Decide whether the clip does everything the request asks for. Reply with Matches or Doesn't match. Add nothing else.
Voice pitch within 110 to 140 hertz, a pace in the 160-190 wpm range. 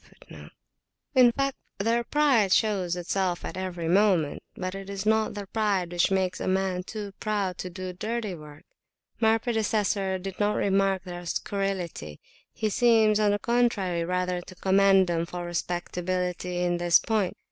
Doesn't match